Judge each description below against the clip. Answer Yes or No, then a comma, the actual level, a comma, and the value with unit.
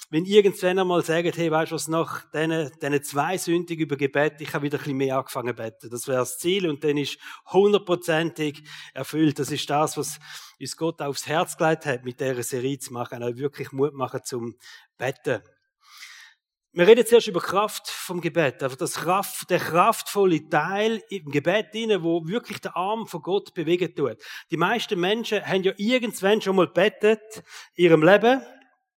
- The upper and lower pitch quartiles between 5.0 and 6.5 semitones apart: Yes, average, 5.3 semitones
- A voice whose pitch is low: No, medium, 165 Hz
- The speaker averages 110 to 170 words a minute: No, average, 185 wpm